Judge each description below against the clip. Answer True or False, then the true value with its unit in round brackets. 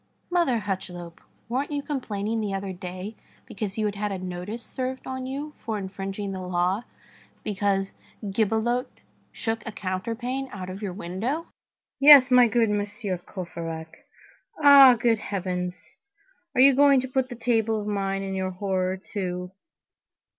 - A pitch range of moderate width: True (4.6 semitones)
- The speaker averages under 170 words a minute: True (150 wpm)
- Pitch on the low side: False (205 Hz)